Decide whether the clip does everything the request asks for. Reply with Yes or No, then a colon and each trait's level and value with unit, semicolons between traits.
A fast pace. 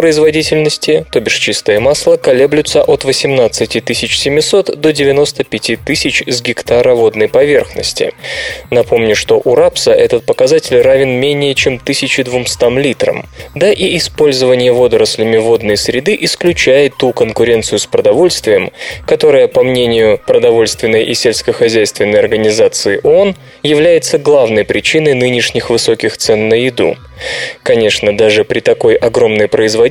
No: average, 120 wpm